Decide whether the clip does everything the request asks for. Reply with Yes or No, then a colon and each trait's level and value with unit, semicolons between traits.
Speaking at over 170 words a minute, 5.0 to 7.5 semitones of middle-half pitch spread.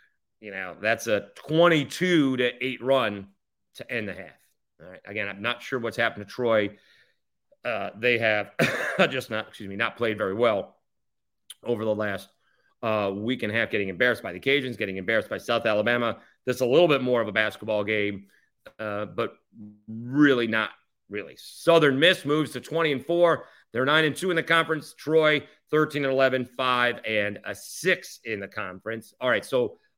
Yes: average, 190 wpm; wide, 5.4 semitones